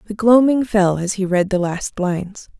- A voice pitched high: Yes, high, 200 Hz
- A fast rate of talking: Yes, fast, 210 wpm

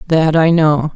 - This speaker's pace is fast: No, average, 190 wpm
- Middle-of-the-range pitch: Yes, medium, 155 Hz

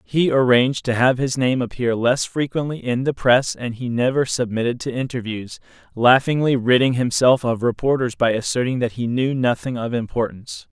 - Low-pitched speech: Yes, low, 125 Hz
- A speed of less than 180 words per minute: Yes, average, 170 wpm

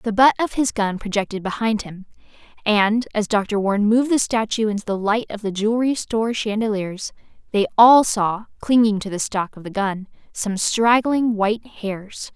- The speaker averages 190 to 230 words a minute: No, average, 180 wpm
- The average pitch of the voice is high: Yes, high, 215 Hz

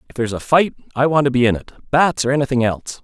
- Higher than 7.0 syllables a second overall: Yes, 7.2 syllables/s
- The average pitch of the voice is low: Yes, low, 130 Hz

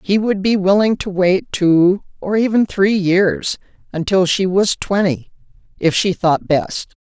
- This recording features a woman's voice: Yes, female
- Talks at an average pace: Yes, average, 160 wpm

